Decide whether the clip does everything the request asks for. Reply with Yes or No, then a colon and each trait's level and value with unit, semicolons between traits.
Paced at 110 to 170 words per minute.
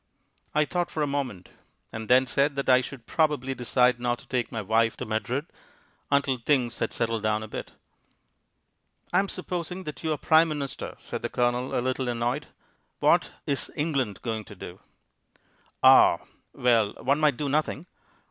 Yes: average, 165 wpm